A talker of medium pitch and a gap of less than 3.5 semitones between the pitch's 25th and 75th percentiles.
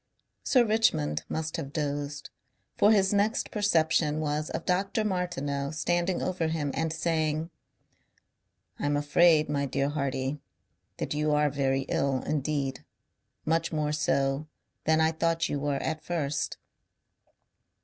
Yes: medium, 155 Hz; average, 2.8 semitones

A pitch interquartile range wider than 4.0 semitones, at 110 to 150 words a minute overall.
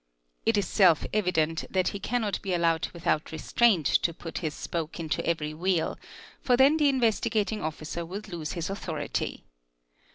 No: average, 4.7 semitones; average, 160 wpm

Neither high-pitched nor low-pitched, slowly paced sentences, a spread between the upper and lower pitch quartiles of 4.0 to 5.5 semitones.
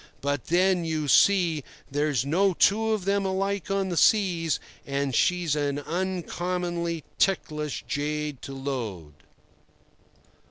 Yes: medium, 165 Hz; slow, 120 wpm; average, 4.6 semitones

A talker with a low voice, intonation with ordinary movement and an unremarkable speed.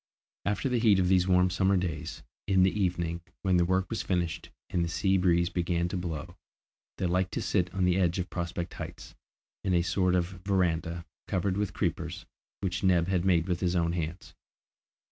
No: very low, 90 Hz; narrow, 1.6 semitones; average, 195 wpm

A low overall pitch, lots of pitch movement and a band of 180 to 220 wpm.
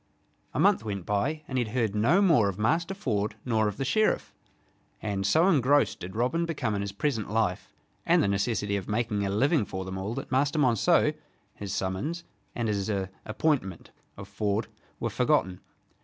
Yes: low, 110 Hz; wide, 5.9 semitones; average, 185 wpm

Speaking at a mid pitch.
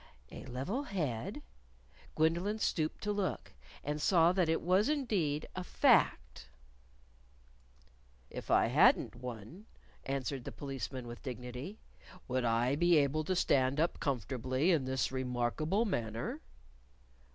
Yes: medium, 145 Hz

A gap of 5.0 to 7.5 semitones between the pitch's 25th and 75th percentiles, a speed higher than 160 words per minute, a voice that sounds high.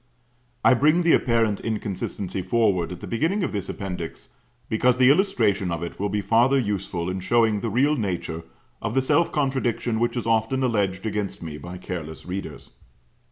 No: average, 5.3 semitones; average, 175 wpm; low, 110 Hz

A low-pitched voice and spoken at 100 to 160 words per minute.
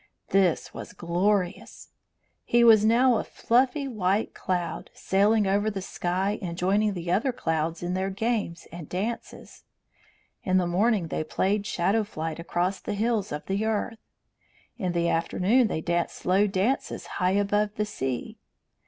No: high, 195 Hz; average, 155 wpm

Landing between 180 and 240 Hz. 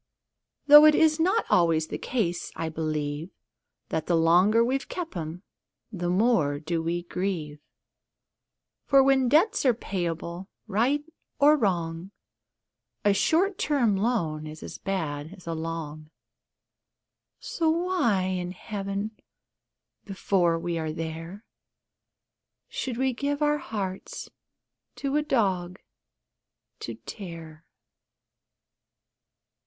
Yes: high, 190 Hz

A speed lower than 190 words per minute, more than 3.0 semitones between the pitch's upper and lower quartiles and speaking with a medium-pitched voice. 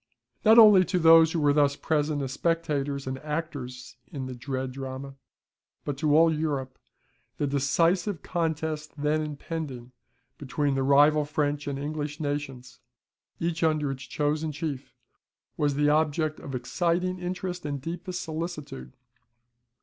No: average, 140 wpm; average, 2.7 semitones; medium, 150 Hz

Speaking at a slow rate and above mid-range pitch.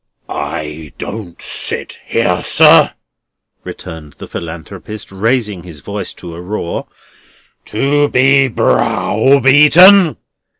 No: slow, 95 wpm; low, 105 Hz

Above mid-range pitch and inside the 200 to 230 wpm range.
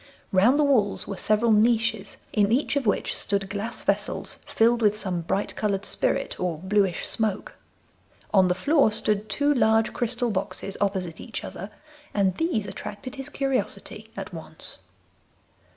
No: high, 210 Hz; average, 150 wpm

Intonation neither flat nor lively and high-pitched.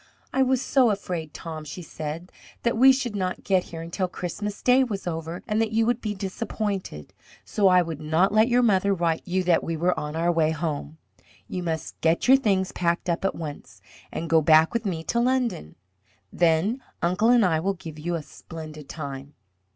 No: average, 4.8 semitones; medium, 180 Hz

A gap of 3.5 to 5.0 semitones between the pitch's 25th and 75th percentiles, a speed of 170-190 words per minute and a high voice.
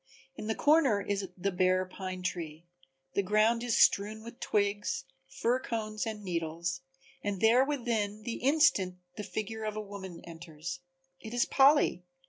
No: average, 3.8 semitones; average, 155 wpm; high, 205 Hz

